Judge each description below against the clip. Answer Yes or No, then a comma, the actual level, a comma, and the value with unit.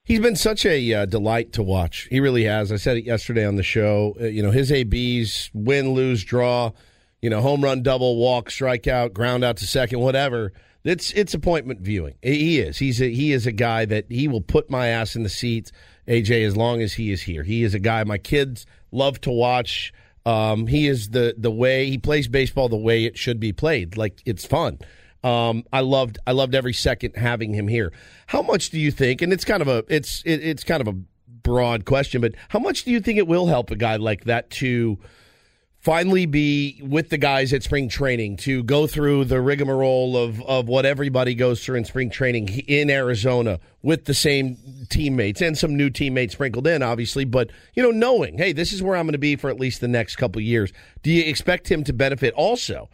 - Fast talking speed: Yes, fast, 225 wpm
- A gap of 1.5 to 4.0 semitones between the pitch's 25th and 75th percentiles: Yes, average, 3.7 semitones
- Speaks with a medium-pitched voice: No, low, 125 Hz